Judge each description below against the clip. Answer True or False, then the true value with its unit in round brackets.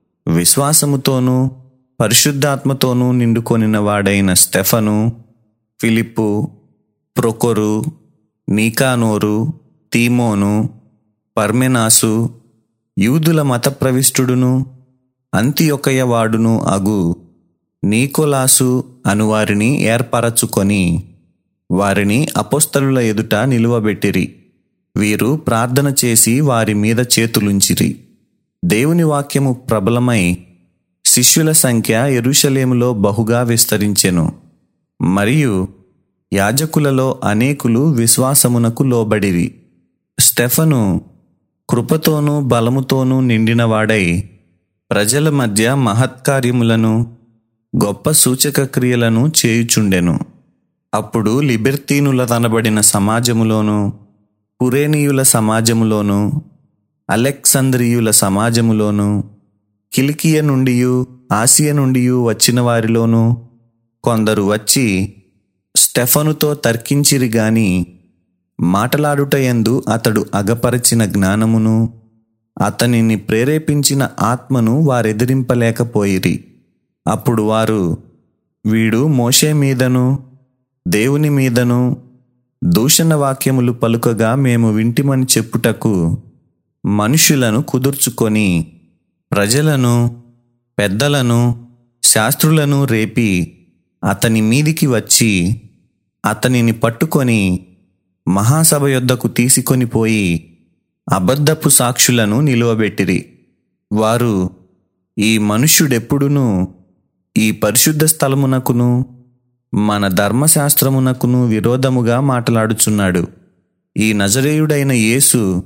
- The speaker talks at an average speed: False (65 wpm)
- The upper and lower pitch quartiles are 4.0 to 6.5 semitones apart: False (3.6 semitones)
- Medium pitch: False (120 Hz)